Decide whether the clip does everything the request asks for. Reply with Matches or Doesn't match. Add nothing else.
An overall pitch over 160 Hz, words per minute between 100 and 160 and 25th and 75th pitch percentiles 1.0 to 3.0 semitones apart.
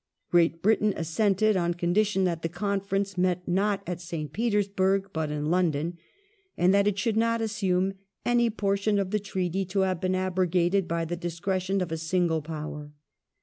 Doesn't match